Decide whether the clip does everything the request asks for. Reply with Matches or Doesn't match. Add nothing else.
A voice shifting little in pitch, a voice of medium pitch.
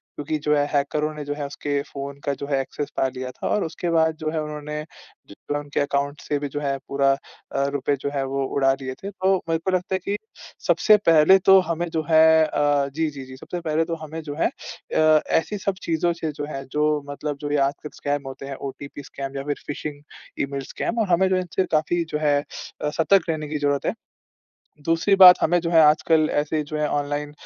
Matches